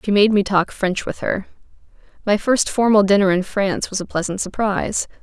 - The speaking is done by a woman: Yes, female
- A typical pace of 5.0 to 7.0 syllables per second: Yes, 5.5 syllables/s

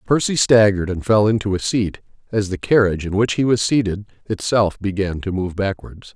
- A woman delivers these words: No, male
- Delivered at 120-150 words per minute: No, average, 195 wpm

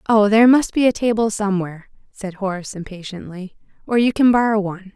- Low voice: No, high, 205 Hz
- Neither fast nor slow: Yes, average, 180 wpm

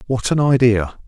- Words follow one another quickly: No, average, 165 wpm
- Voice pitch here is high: No, low, 120 Hz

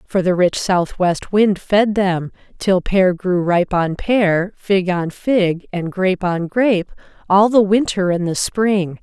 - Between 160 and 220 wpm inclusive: Yes, average, 175 wpm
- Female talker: Yes, female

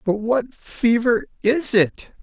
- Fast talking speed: No, slow, 135 wpm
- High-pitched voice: Yes, high, 230 Hz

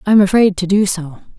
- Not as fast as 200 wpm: No, fast, 260 wpm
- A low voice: No, high, 190 Hz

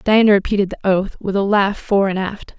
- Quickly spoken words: Yes, fast, 230 wpm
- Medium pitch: No, high, 200 Hz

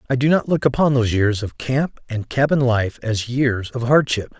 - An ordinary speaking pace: No, fast, 220 wpm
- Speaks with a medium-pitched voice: No, low, 125 Hz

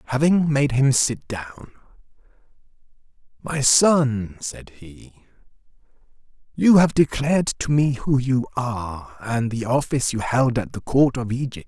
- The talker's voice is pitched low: Yes, low, 130 Hz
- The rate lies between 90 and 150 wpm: Yes, average, 140 wpm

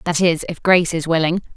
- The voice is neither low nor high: Yes, medium, 165 Hz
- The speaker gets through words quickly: Yes, fast, 230 wpm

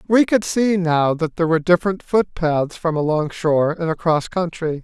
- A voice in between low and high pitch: Yes, medium, 170 Hz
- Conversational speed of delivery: Yes, average, 185 wpm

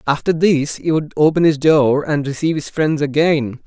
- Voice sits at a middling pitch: Yes, medium, 150 Hz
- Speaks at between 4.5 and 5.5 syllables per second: Yes, 4.9 syllables/s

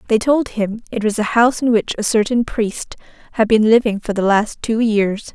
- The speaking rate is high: Yes, fast, 225 wpm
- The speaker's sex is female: Yes, female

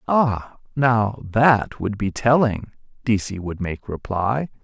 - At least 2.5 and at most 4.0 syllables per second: Yes, 3.3 syllables/s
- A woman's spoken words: No, male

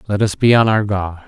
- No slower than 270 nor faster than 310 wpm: Yes, fast, 280 wpm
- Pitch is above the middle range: No, low, 100 Hz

